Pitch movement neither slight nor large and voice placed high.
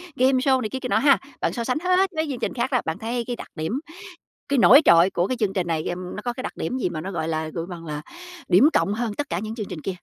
No: wide, 6.7 semitones; high, 220 Hz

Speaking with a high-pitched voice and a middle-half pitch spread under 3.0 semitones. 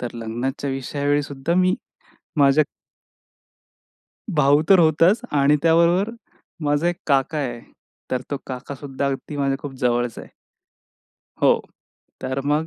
No: medium, 140 Hz; narrow, 2.6 semitones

